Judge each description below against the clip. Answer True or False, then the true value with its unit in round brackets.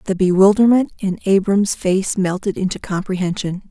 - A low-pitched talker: False (190 Hz)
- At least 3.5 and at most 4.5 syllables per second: False (5.0 syllables/s)